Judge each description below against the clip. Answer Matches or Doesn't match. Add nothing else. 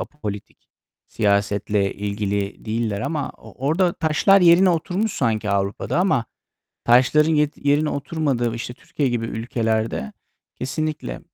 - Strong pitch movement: Matches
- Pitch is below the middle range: Matches